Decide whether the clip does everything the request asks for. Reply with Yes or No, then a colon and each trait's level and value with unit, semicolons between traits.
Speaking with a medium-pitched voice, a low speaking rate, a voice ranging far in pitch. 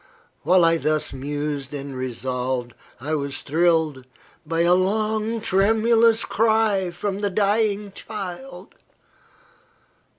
Yes: medium, 175 Hz; slow, 105 wpm; wide, 6.7 semitones